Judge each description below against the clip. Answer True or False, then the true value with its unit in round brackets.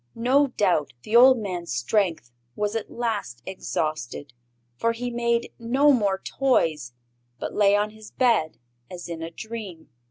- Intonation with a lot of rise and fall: True (6.3 semitones)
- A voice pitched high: True (210 Hz)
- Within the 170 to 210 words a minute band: False (150 wpm)